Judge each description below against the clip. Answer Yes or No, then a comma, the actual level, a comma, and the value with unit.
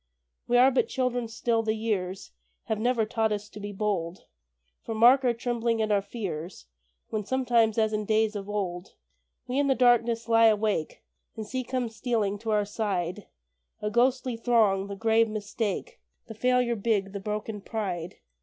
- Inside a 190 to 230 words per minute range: No, average, 175 wpm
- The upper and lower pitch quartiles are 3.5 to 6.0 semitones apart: No, narrow, 2.5 semitones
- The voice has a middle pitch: No, high, 220 Hz